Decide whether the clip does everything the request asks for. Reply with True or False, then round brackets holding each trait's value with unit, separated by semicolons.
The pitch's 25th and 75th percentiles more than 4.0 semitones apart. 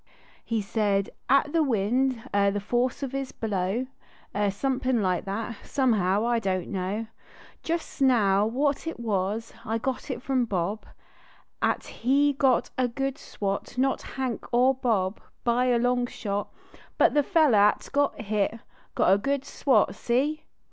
True (4.6 semitones)